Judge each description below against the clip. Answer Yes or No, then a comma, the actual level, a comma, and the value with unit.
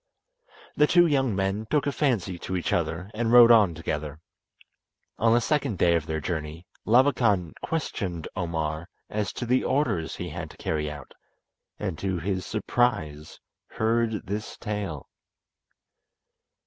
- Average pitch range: No, wide, 6.1 semitones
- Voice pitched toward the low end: Yes, very low, 95 Hz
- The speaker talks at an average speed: Yes, average, 145 wpm